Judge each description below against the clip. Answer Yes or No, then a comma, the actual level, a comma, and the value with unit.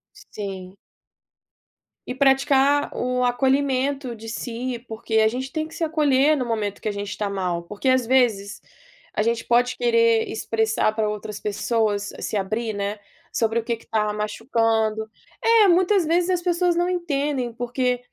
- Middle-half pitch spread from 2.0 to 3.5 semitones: No, average, 4.1 semitones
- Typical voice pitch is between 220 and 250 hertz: Yes, high, 235 Hz